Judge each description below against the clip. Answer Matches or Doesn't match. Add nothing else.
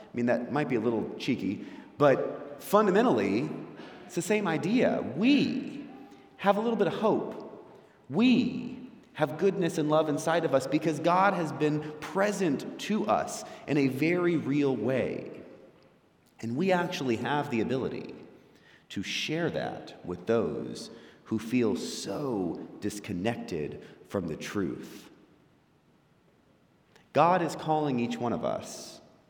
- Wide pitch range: Matches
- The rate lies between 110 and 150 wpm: Matches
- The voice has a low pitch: Doesn't match